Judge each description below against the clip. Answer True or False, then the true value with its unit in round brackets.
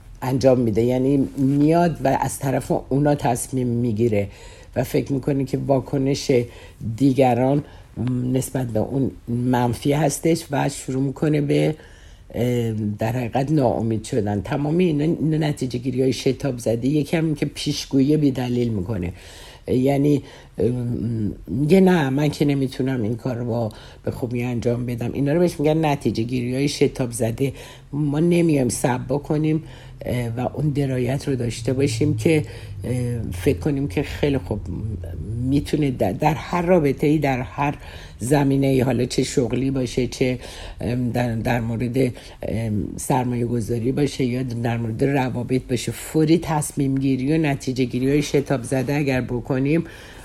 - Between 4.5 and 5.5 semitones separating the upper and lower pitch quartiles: False (3.2 semitones)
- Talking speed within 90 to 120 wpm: False (140 wpm)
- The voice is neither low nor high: False (130 Hz)